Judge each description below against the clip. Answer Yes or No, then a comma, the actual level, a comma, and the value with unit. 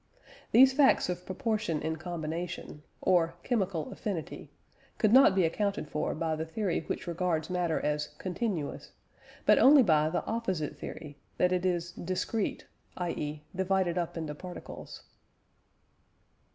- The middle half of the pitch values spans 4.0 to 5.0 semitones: No, average, 3.3 semitones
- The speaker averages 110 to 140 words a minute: Yes, slow, 135 wpm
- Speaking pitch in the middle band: Yes, medium, 175 Hz